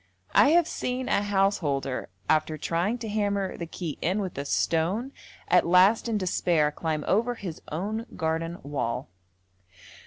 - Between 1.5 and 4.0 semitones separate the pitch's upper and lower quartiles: No, average, 4.9 semitones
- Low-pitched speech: No, medium, 180 Hz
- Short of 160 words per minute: Yes, average, 150 wpm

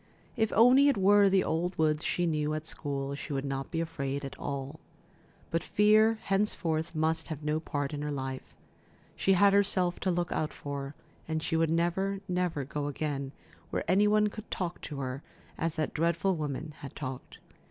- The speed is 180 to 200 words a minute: Yes, average, 190 wpm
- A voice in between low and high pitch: Yes, medium, 160 Hz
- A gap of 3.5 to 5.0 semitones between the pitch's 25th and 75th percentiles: Yes, average, 4.6 semitones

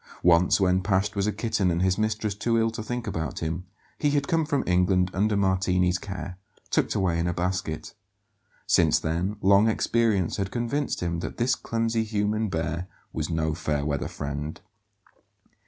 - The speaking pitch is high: No, very low, 95 Hz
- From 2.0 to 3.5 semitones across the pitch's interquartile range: No, average, 4.1 semitones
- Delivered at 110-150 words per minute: No, average, 170 wpm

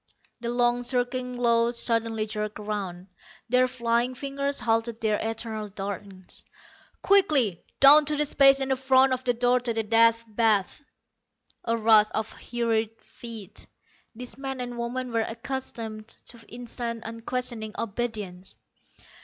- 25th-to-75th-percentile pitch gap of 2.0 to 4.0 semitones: Yes, narrow, 2.4 semitones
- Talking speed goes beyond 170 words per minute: No, slow, 135 wpm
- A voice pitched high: Yes, high, 235 Hz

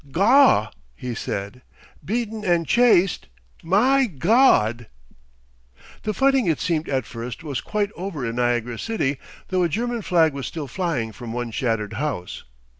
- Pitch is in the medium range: Yes, medium, 160 Hz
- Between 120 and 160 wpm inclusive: Yes, average, 145 wpm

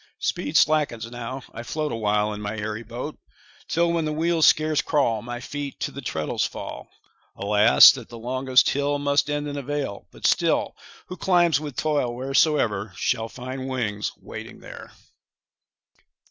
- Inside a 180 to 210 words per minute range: No, average, 165 wpm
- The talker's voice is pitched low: Yes, low, 130 Hz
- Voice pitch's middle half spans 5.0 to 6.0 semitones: No, average, 4.6 semitones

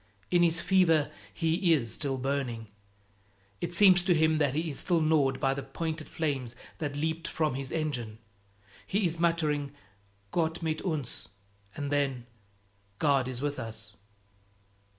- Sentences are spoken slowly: No, average, 150 wpm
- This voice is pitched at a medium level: Yes, medium, 150 Hz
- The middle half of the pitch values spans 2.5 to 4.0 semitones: Yes, average, 3.5 semitones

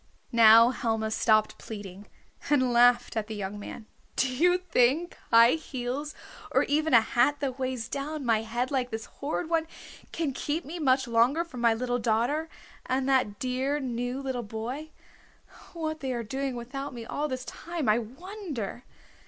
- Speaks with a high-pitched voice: Yes, very high, 255 Hz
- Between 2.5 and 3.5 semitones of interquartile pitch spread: No, average, 3.9 semitones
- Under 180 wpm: Yes, average, 170 wpm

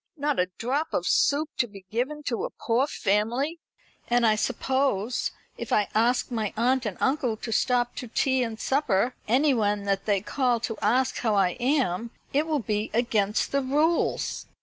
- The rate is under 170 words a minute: No, average, 175 wpm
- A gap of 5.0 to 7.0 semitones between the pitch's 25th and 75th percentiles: No, average, 4.0 semitones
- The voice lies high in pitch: Yes, high, 240 Hz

